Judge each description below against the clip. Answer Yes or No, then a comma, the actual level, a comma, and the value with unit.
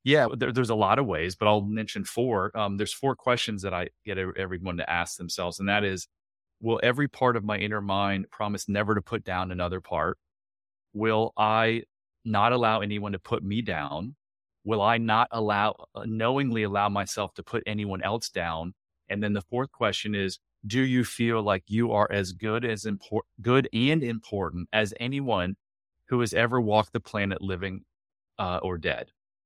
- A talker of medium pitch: No, low, 105 Hz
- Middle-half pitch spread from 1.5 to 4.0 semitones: Yes, average, 3.1 semitones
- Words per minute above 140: Yes, average, 185 wpm